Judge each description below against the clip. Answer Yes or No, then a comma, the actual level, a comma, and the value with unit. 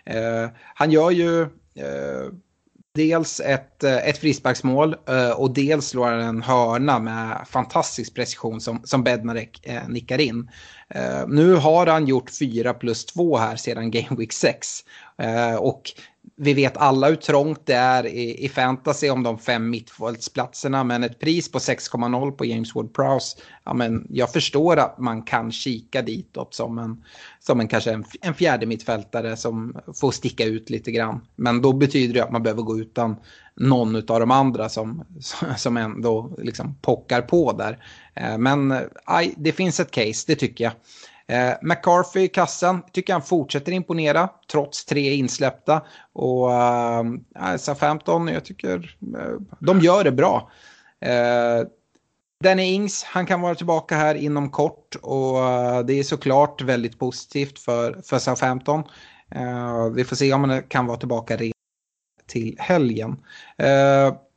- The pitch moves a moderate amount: Yes, average, 4.2 semitones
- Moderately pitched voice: No, low, 130 Hz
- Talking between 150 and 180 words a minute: Yes, average, 155 wpm